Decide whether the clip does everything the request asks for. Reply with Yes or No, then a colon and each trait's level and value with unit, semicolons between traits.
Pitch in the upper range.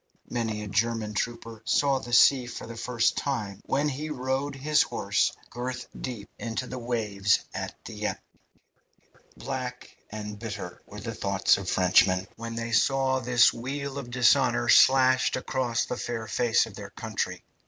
No: low, 120 Hz